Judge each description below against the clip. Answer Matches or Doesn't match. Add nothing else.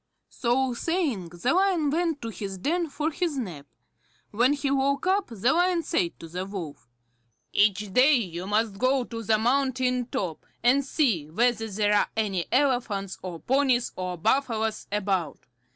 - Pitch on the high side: Matches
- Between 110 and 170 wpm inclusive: Matches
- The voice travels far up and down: Matches